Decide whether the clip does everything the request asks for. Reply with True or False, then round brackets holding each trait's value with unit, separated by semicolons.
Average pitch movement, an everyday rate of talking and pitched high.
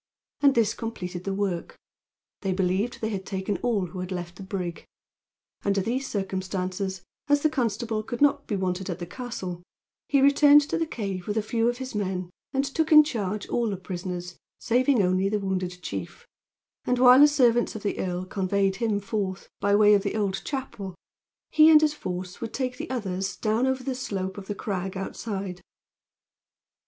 True (4.6 semitones; 190 wpm; 200 Hz)